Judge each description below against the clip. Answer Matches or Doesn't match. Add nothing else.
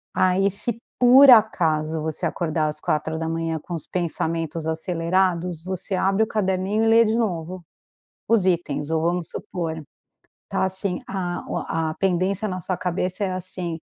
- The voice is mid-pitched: Matches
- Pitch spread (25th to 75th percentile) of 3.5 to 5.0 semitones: Doesn't match